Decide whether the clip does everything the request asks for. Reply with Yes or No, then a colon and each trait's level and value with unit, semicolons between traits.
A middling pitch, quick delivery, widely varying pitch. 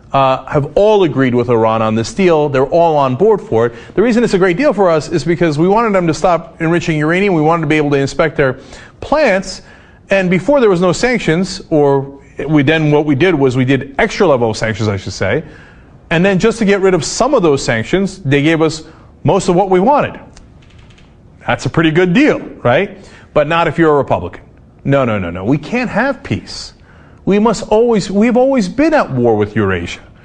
Yes: medium, 160 Hz; fast, 220 wpm; wide, 6.2 semitones